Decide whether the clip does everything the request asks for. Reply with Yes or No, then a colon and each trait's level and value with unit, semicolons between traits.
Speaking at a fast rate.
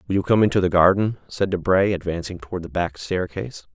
Yes: fast, 210 wpm